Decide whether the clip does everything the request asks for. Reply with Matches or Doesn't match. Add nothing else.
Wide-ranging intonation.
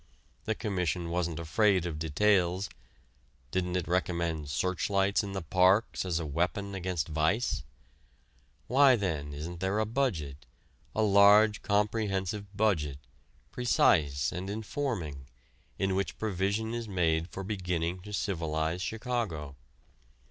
Doesn't match